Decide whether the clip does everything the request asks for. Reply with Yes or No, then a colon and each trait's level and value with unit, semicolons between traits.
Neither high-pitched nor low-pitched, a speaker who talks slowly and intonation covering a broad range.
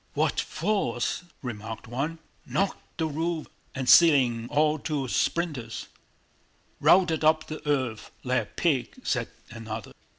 No: medium, 145 Hz; slow, 125 wpm; average, 5.0 semitones